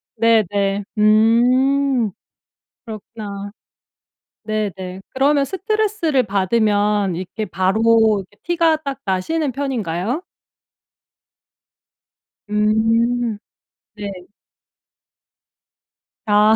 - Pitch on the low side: No, high, 220 Hz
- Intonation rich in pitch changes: No, average, 4.6 semitones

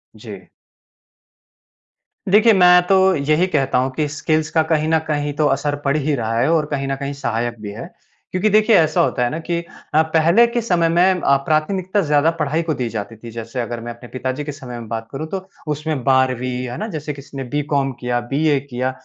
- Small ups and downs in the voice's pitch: No, average, 4.1 semitones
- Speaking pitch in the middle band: Yes, medium, 145 Hz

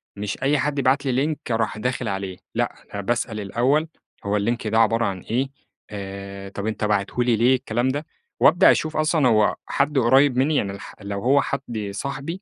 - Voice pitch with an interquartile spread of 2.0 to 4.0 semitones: No, average, 5.1 semitones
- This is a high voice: No, low, 120 Hz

